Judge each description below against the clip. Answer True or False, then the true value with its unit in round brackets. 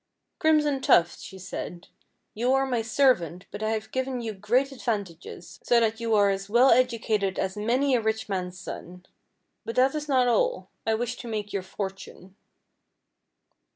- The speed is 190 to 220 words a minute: False (170 wpm)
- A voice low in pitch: False (220 Hz)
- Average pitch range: True (4.6 semitones)